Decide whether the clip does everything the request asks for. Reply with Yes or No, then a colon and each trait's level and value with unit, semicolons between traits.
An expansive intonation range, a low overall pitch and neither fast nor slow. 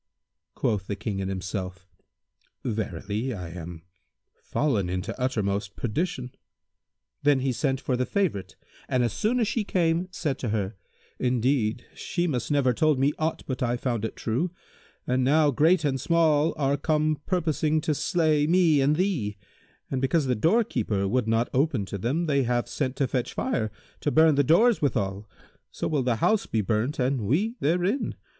Yes: wide, 6.1 semitones; low, 130 Hz; average, 170 wpm